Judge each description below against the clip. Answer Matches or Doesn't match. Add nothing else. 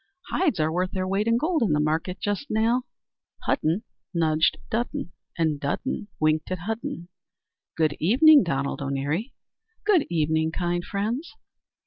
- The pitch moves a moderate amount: Doesn't match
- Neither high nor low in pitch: Matches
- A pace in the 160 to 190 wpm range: Doesn't match